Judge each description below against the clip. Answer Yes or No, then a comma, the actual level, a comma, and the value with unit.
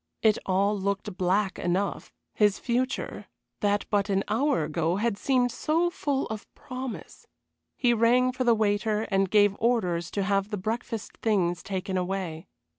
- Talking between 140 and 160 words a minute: Yes, average, 155 wpm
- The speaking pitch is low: No, high, 205 Hz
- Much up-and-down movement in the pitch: No, average, 3.6 semitones